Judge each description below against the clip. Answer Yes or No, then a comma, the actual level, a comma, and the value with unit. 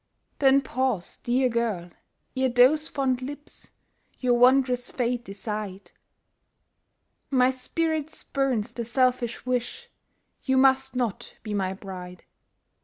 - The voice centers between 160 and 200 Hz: No, very high, 250 Hz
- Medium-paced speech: No, slow, 110 wpm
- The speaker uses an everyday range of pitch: Yes, average, 3.1 semitones